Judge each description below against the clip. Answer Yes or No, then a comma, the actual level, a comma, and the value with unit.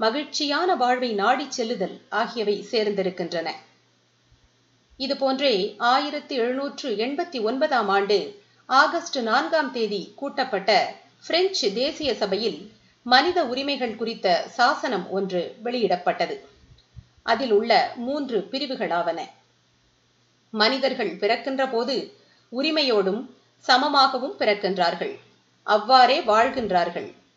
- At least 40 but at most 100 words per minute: Yes, average, 80 wpm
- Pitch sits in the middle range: No, high, 245 Hz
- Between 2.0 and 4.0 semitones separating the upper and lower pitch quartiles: No, average, 5.2 semitones